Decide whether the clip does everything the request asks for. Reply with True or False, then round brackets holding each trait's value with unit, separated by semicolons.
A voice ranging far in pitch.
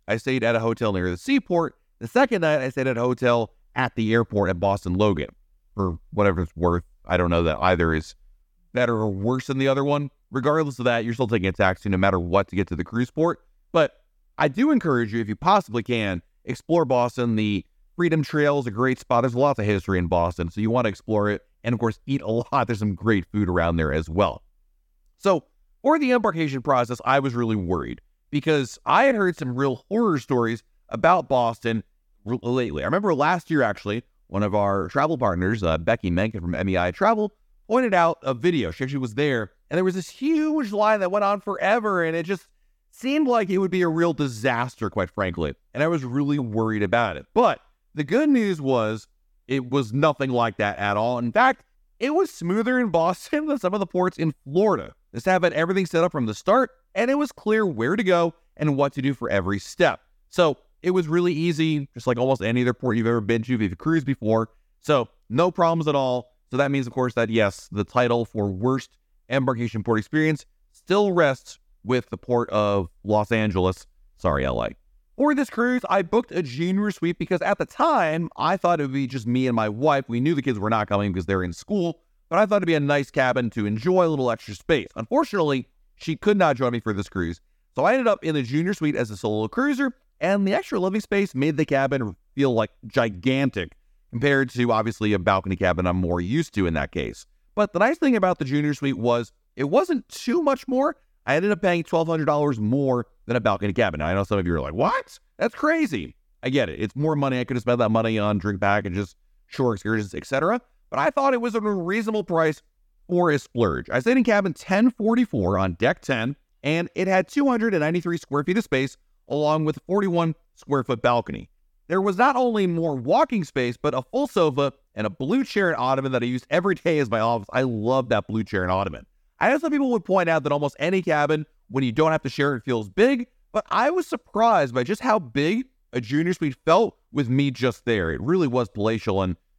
True (8.4 semitones)